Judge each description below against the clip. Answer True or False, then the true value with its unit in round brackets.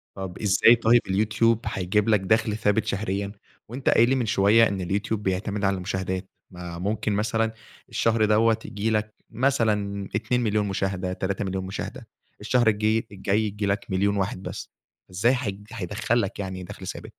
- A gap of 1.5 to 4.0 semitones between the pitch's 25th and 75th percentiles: True (2.4 semitones)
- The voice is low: True (105 Hz)